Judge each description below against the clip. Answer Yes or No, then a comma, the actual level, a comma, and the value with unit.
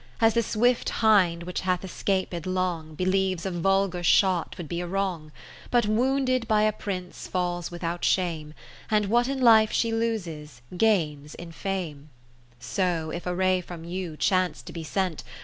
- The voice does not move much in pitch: No, average, 3.7 semitones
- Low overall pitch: No, medium, 185 Hz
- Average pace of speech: Yes, average, 175 wpm